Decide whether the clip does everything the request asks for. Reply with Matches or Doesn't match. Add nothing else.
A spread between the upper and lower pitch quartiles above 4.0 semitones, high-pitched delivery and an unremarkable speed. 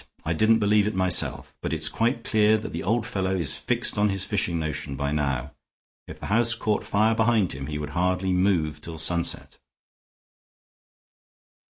Doesn't match